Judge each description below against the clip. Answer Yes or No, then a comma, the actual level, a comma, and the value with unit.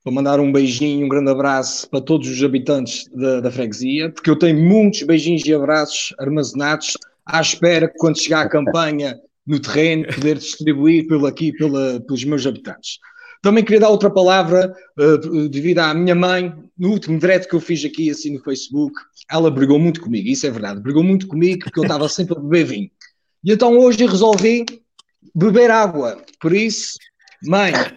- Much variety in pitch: No, average, 4.2 semitones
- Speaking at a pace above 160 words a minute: Yes, average, 180 wpm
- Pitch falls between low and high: Yes, medium, 160 Hz